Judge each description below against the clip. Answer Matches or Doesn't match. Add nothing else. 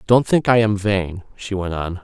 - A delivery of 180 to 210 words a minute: Doesn't match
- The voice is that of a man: Matches